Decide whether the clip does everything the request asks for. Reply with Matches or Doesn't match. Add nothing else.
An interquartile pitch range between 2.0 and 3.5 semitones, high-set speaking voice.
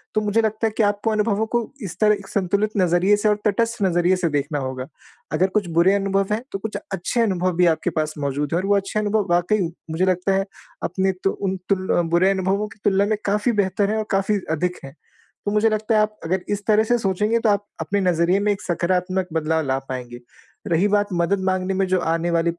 Matches